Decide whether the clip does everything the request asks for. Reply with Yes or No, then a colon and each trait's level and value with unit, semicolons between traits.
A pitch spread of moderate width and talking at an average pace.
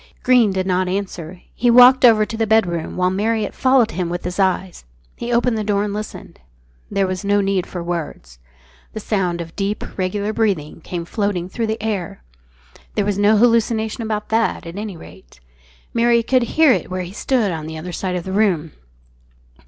Yes: average, 3.6 semitones; average, 190 wpm